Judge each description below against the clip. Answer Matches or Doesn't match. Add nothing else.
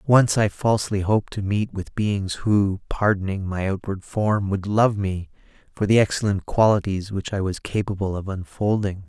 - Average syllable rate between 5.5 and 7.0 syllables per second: Doesn't match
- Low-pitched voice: Matches